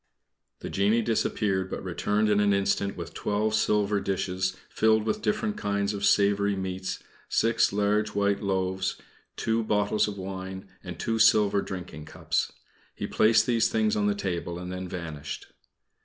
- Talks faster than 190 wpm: No, average, 155 wpm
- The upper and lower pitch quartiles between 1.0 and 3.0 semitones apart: Yes, narrow, 2.4 semitones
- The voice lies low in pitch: Yes, low, 100 Hz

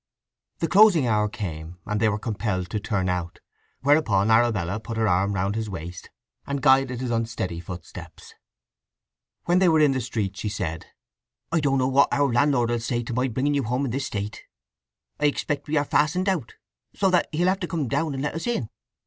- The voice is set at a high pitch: No, low, 120 Hz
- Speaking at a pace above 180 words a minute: Yes, fast, 205 wpm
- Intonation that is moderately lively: No, wide, 6.0 semitones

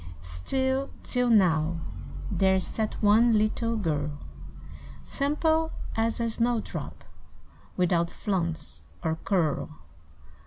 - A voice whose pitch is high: Yes, high, 205 Hz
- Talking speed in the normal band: No, slow, 95 wpm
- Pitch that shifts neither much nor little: No, wide, 6.3 semitones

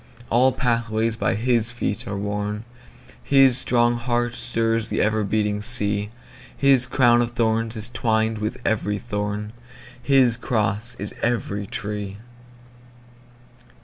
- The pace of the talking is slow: Yes, slow, 115 wpm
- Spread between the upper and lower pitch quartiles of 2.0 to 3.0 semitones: Yes, narrow, 2.5 semitones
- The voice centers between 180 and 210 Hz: No, low, 115 Hz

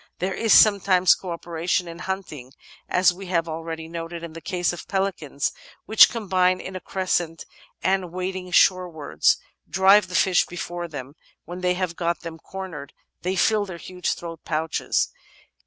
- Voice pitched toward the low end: No, medium, 180 Hz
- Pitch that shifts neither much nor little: No, narrow, 2.2 semitones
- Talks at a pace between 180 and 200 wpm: No, average, 165 wpm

